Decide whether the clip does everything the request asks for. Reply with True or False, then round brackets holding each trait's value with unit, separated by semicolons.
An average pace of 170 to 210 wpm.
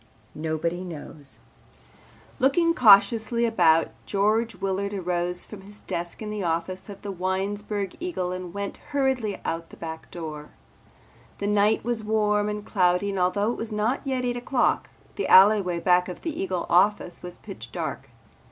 False (160 wpm)